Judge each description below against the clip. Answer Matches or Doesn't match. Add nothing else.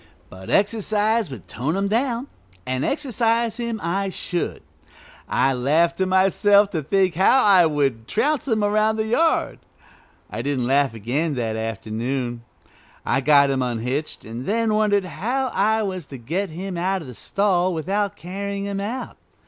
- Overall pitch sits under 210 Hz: Matches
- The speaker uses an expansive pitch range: Matches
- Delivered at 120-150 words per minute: Doesn't match